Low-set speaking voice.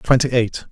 Yes: low, 125 Hz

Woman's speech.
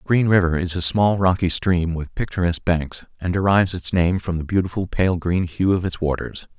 No: male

